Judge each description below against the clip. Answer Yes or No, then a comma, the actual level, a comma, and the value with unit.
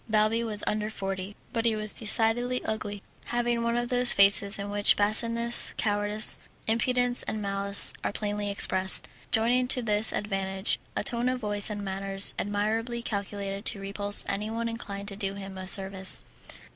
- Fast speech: No, average, 160 wpm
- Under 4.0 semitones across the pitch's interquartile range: Yes, narrow, 2.5 semitones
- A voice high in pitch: Yes, high, 210 Hz